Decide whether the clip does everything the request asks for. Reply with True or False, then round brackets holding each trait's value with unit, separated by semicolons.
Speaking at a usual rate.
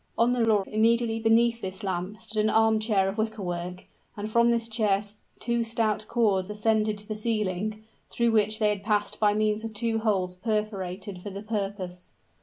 True (180 wpm)